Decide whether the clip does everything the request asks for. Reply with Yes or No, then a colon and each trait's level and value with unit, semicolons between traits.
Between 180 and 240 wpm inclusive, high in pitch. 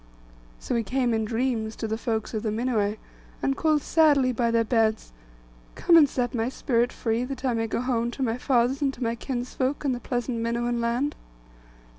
Yes: average, 200 wpm; high, 240 Hz